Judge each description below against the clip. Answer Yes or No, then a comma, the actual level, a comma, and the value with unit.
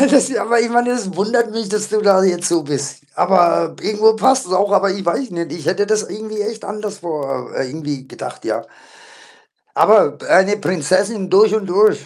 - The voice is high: Yes, high, 200 Hz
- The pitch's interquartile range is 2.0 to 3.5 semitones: No, average, 3.9 semitones